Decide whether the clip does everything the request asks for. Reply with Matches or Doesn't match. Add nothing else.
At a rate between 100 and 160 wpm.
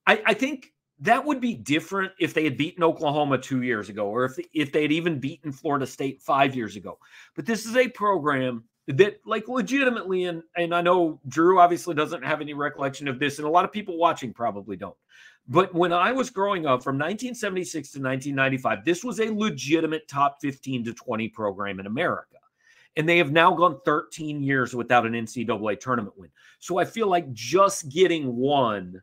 Doesn't match